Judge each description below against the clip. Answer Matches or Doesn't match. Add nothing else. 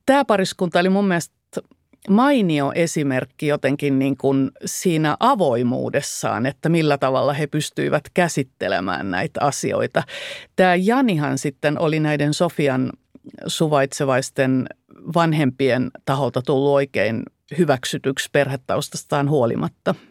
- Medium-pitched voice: Matches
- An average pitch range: Matches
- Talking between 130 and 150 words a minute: Doesn't match